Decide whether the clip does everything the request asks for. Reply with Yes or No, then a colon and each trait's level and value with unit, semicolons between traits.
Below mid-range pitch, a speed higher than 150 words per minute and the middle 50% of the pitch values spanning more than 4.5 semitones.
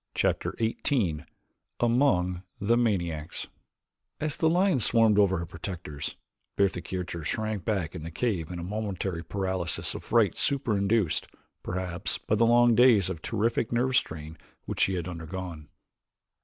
No: very low, 95 Hz; average, 145 wpm; average, 5.1 semitones